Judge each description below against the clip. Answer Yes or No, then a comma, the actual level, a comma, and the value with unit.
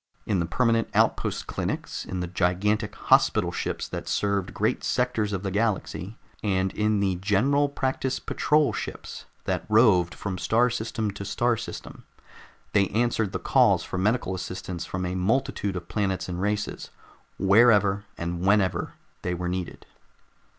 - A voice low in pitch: Yes, low, 100 Hz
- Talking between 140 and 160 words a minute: Yes, average, 150 wpm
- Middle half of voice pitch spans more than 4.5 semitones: No, average, 3.2 semitones